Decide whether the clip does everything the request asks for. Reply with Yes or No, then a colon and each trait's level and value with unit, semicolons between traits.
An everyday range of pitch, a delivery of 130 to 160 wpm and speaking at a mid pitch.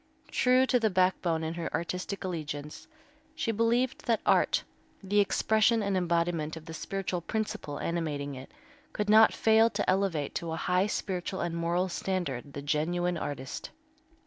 Yes: average, 4.2 semitones; average, 155 wpm; medium, 180 Hz